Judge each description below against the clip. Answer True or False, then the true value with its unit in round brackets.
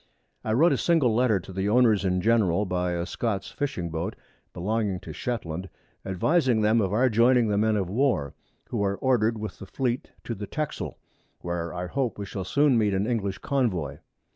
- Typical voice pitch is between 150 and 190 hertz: False (105 Hz)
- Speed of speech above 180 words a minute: True (190 wpm)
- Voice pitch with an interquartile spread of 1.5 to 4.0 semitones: False (4.6 semitones)